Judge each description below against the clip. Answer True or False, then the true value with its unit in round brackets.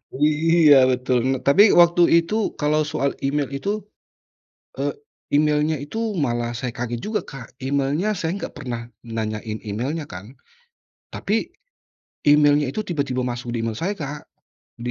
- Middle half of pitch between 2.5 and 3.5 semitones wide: False (4.0 semitones)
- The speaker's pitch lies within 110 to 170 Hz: True (140 Hz)